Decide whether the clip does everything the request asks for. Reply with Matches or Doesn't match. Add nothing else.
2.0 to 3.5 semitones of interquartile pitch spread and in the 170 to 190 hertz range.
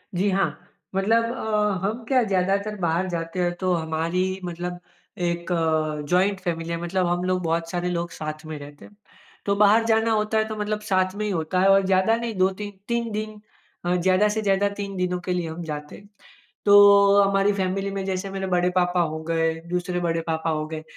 Matches